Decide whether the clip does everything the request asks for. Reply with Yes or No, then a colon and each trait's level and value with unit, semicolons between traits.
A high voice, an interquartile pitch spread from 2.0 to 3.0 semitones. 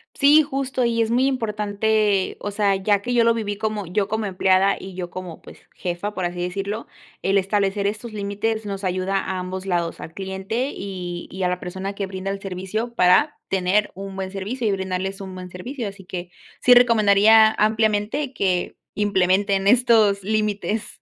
Yes: high, 200 Hz; narrow, 2.6 semitones